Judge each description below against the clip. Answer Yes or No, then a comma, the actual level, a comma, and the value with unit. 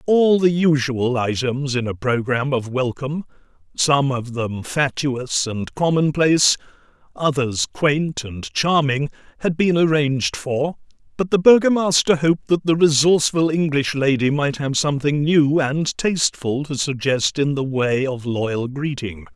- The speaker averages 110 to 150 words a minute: Yes, average, 145 wpm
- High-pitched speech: No, medium, 140 Hz